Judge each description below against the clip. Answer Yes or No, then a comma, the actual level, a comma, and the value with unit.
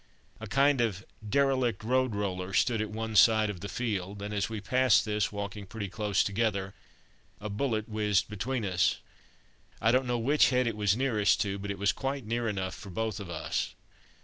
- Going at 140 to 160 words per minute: No, average, 195 wpm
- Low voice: Yes, low, 105 Hz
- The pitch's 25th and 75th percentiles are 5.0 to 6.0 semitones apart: No, average, 2.9 semitones